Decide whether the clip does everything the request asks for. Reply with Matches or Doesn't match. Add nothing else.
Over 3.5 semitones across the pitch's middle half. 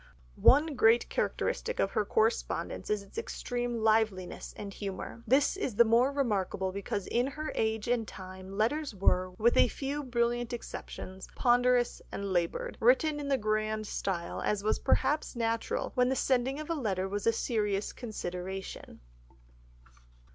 Matches